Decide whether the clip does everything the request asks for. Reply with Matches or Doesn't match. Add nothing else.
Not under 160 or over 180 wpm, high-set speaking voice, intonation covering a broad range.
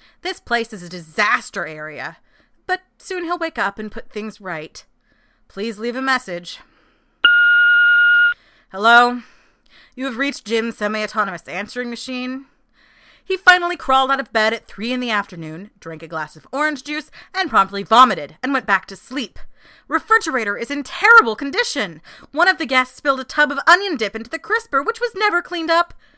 Matches